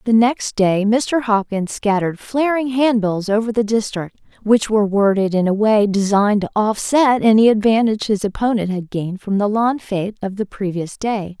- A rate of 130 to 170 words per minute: No, average, 185 wpm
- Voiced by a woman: Yes, female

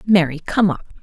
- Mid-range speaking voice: Yes, medium, 180 Hz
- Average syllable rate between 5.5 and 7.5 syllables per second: No, 5.1 syllables/s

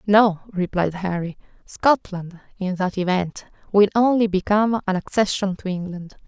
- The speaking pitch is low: No, high, 195 Hz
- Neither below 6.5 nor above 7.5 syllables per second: No, 4.6 syllables/s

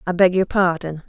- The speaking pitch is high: No, medium, 175 Hz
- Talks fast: Yes, fast, 220 wpm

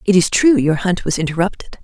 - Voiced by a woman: Yes, female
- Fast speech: Yes, fast, 230 wpm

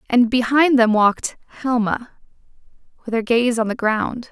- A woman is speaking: Yes, female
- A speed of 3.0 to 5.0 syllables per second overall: Yes, 4.8 syllables/s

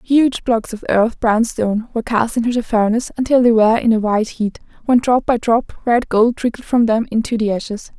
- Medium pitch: No, high, 230 Hz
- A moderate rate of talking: No, fast, 225 wpm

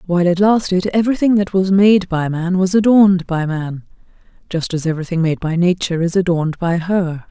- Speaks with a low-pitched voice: No, medium, 180 Hz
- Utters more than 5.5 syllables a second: Yes, 5.8 syllables/s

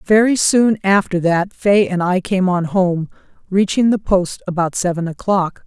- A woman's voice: Yes, female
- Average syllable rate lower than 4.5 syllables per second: Yes, 4.3 syllables/s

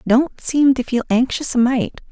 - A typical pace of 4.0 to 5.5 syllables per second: Yes, 4.3 syllables/s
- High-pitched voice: Yes, very high, 255 Hz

